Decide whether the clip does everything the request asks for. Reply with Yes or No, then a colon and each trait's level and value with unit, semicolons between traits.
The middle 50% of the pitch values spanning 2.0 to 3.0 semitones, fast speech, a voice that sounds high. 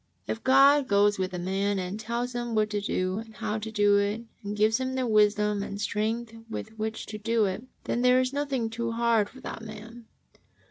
Yes: narrow, 2.4 semitones; fast, 215 wpm; high, 220 Hz